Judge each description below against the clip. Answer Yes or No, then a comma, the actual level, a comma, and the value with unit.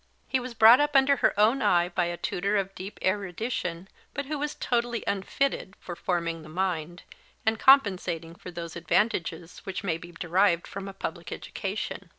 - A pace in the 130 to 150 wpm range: No, average, 175 wpm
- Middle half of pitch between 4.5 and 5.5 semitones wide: Yes, average, 5.1 semitones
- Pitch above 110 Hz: Yes, high, 190 Hz